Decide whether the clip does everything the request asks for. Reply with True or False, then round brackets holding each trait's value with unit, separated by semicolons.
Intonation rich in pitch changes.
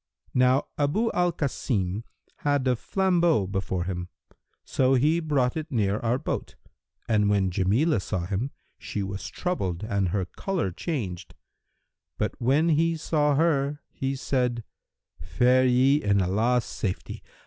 True (7.0 semitones)